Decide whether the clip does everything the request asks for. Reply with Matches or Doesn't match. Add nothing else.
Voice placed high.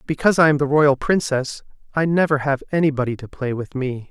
Doesn't match